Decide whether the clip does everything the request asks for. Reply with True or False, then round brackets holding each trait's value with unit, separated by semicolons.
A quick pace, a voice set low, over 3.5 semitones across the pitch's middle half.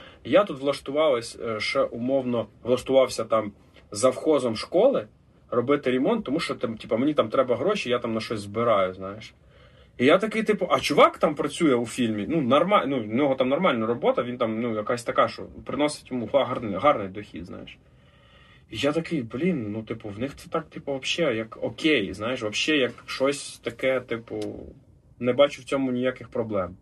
True (180 wpm; 125 Hz; 3.9 semitones)